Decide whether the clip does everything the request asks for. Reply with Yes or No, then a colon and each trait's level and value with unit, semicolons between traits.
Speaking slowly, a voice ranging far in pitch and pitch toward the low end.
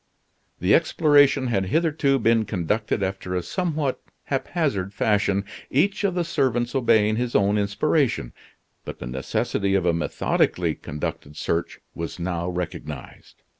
Yes: slow, 130 wpm; wide, 7.2 semitones; low, 105 Hz